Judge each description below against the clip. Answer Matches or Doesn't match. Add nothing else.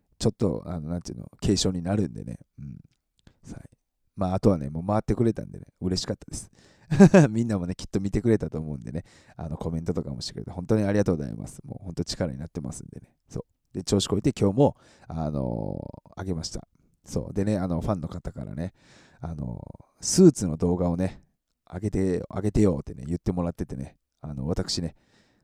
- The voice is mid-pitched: Doesn't match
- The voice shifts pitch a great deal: Doesn't match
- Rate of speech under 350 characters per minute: Doesn't match